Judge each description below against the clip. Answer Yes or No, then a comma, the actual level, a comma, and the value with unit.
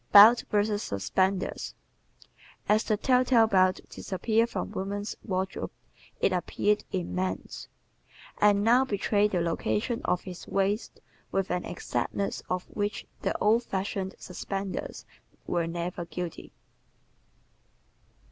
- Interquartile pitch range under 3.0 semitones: Yes, narrow, 2.5 semitones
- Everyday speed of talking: No, slow, 120 wpm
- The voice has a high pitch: Yes, high, 195 Hz